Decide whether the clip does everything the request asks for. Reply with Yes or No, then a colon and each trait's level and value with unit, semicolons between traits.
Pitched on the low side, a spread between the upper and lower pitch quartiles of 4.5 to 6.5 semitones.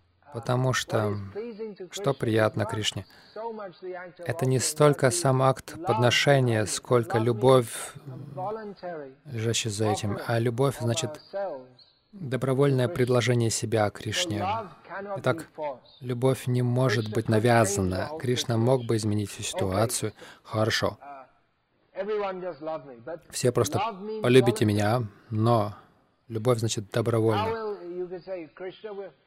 Yes: low, 125 Hz; average, 5.2 semitones